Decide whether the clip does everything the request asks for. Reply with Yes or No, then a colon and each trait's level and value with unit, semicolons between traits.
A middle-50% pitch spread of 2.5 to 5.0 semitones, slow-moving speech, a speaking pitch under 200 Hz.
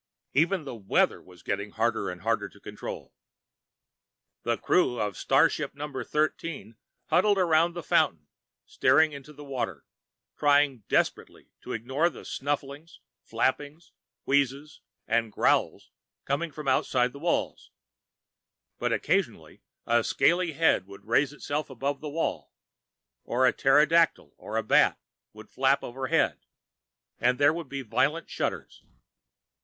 Yes: average, 4.5 semitones; slow, 130 wpm; medium, 140 Hz